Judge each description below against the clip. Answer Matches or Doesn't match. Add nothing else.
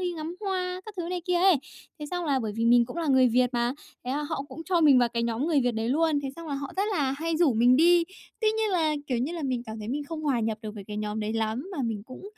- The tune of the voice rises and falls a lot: Matches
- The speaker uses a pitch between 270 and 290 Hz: Matches